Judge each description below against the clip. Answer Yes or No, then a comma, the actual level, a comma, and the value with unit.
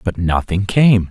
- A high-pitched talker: No, low, 100 Hz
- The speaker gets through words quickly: No, average, 165 wpm